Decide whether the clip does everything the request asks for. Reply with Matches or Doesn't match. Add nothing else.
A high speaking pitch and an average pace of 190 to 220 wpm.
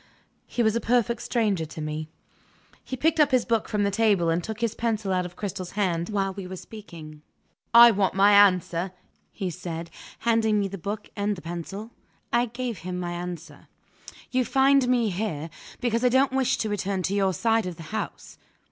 Matches